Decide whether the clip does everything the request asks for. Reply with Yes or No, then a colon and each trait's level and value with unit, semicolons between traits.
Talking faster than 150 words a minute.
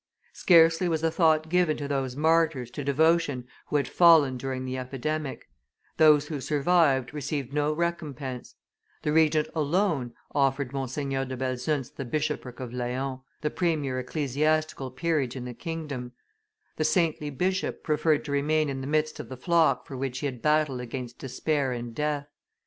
Yes: average, 160 wpm